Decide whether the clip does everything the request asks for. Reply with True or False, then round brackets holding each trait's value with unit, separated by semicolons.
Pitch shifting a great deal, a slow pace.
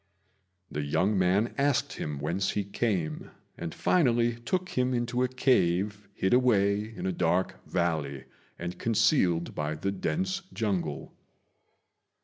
True (5.9 semitones; 130 wpm)